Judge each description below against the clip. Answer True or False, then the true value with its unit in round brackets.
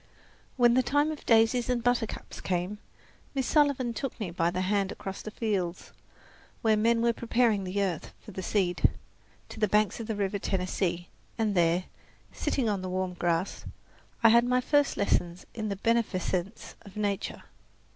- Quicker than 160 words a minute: True (170 wpm)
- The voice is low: False (210 Hz)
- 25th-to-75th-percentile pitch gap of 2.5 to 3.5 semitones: False (4.0 semitones)